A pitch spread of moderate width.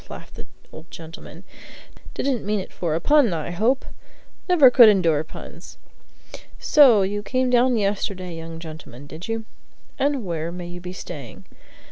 No: wide, 6.6 semitones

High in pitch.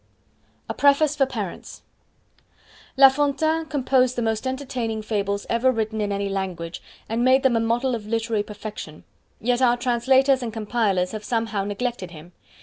Yes: high, 230 Hz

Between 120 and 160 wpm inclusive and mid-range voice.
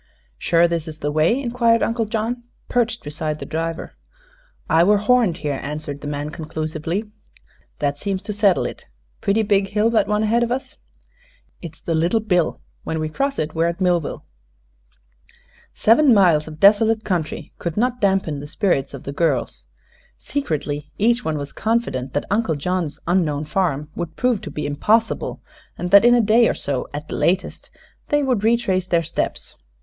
No: average, 175 wpm; medium, 180 Hz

